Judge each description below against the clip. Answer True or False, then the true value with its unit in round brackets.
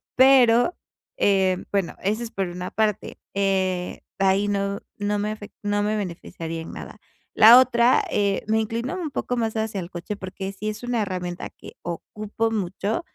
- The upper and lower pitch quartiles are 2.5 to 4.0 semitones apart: True (2.9 semitones)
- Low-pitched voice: False (205 Hz)